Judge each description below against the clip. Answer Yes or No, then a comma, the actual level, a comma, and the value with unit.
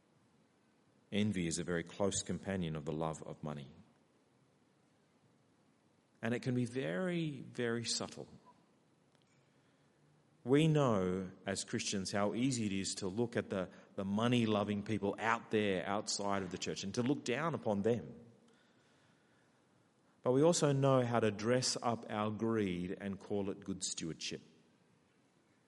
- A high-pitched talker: No, low, 105 Hz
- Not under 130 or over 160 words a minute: Yes, average, 145 wpm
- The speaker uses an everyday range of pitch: Yes, average, 3.9 semitones